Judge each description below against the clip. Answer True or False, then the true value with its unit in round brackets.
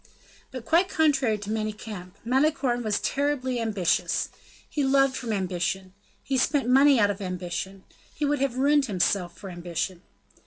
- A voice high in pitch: True (230 Hz)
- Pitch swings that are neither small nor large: False (6.1 semitones)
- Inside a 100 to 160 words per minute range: True (155 wpm)